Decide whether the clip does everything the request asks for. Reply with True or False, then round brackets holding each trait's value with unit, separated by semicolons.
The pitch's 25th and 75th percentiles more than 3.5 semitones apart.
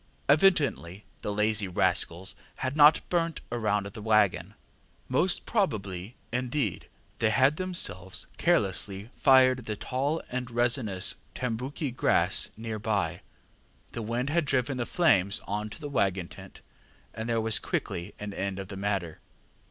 True (4.8 semitones)